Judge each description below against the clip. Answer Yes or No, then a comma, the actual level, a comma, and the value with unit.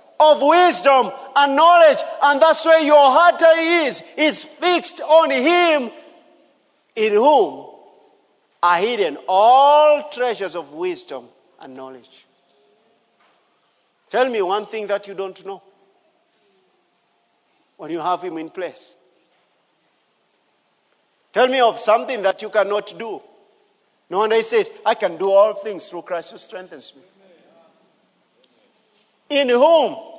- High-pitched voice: Yes, very high, 280 Hz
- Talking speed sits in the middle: No, slow, 120 wpm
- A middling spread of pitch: No, wide, 8.8 semitones